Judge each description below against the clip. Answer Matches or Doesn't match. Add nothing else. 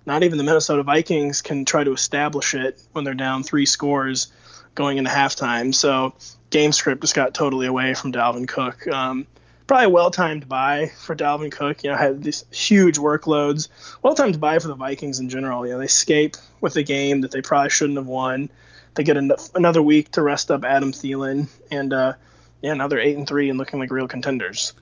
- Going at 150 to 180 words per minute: Doesn't match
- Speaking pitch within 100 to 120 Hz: Doesn't match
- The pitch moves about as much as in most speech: Doesn't match